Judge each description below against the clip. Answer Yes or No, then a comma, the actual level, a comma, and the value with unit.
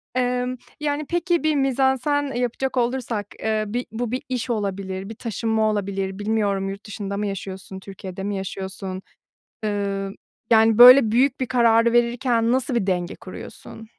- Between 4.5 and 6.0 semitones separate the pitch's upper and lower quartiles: No, average, 4.1 semitones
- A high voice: Yes, high, 225 Hz